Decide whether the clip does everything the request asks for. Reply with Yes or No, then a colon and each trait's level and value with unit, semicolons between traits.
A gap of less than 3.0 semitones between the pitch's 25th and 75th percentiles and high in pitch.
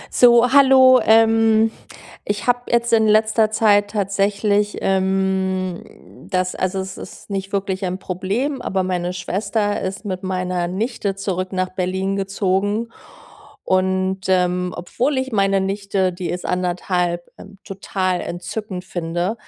Yes: narrow, 2.6 semitones; high, 195 Hz